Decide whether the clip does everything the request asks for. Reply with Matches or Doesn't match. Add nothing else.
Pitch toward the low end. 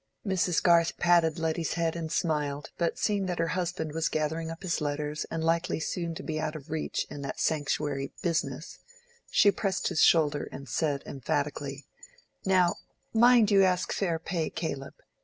Doesn't match